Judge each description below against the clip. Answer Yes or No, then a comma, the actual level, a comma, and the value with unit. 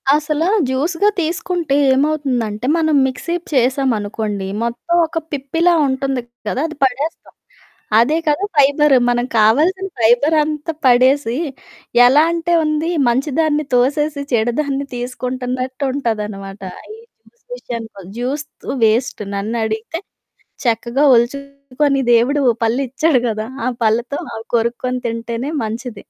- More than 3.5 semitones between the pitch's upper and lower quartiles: Yes, average, 4.2 semitones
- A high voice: Yes, very high, 260 Hz